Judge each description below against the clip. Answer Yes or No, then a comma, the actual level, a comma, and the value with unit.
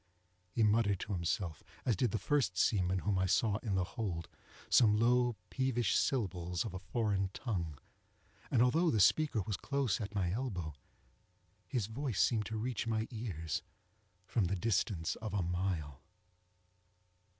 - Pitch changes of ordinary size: Yes, average, 4.4 semitones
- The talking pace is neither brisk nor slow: Yes, average, 155 wpm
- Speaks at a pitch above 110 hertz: No, low, 105 Hz